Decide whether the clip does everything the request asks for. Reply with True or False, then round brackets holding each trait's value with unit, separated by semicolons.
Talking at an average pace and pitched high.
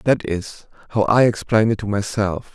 False (190 wpm; 105 Hz)